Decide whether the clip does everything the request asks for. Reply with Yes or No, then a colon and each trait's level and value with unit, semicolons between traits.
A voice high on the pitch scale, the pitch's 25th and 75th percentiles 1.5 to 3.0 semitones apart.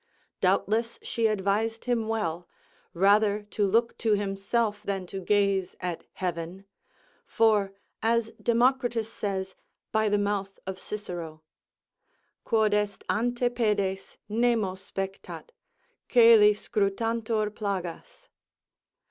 Yes: high, 210 Hz; average, 2.7 semitones